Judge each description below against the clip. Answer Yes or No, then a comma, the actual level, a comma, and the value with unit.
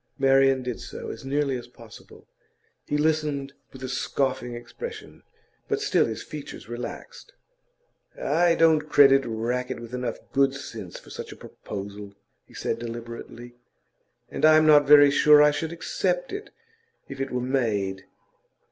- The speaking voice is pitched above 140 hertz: No, low, 135 Hz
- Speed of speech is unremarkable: Yes, average, 150 wpm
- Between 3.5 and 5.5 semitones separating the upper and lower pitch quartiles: Yes, average, 3.9 semitones